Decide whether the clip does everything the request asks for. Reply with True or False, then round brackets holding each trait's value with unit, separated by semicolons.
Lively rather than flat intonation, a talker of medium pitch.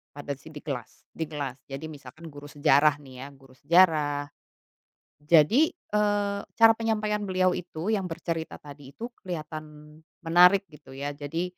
False (4.3 semitones; 155 Hz)